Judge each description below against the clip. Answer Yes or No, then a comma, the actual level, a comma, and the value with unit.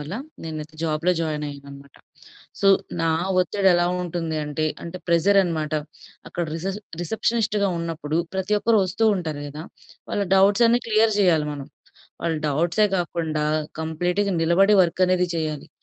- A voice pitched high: No, medium, 170 Hz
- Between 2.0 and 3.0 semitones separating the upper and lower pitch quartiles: No, average, 3.9 semitones